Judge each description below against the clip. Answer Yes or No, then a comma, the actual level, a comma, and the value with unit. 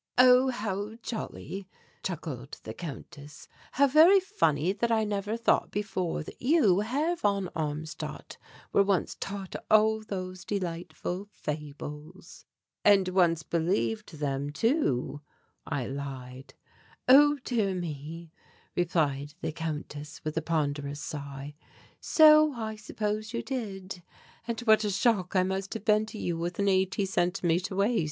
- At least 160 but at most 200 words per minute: No, slow, 135 wpm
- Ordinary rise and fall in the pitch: No, wide, 5.7 semitones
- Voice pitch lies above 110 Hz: Yes, medium, 185 Hz